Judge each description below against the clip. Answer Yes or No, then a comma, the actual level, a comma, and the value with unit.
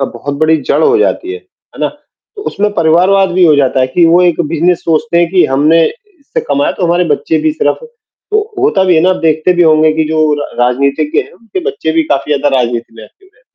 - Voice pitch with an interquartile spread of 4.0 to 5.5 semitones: Yes, average, 4.4 semitones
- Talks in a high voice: No, medium, 165 Hz